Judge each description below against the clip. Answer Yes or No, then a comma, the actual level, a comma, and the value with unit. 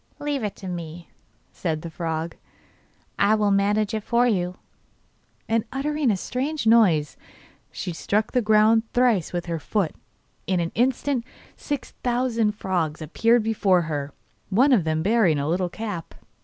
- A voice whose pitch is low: No, high, 205 Hz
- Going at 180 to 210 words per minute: No, average, 155 wpm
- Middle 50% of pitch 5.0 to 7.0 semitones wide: Yes, wide, 5.5 semitones